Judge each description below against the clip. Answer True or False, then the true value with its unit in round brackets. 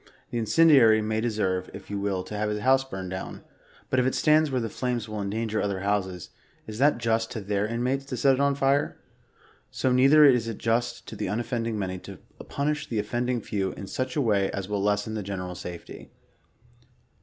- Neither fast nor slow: False (210 wpm)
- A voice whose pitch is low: True (110 Hz)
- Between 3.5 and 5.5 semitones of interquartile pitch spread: True (4.0 semitones)